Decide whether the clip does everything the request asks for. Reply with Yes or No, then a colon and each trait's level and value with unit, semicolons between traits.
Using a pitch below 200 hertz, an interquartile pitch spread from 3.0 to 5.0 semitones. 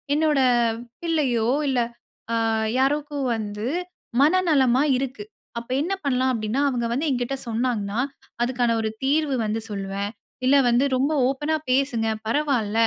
No: very high, 255 Hz; average, 3.9 semitones